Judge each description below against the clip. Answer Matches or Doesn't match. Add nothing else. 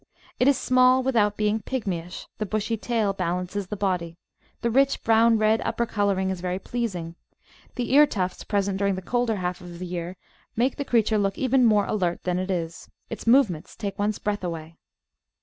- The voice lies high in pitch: Matches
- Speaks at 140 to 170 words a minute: Doesn't match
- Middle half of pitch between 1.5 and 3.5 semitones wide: Doesn't match